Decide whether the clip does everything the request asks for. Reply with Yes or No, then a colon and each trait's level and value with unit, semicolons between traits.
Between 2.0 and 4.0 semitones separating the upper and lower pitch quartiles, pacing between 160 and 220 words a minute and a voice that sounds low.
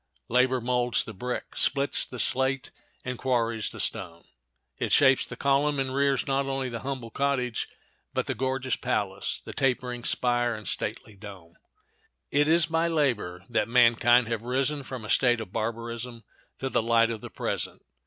Yes: average, 2.8 semitones; average, 170 wpm; low, 125 Hz